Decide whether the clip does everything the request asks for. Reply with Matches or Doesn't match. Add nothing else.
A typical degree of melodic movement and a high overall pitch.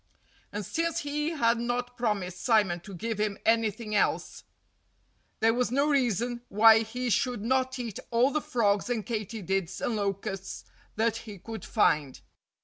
Matches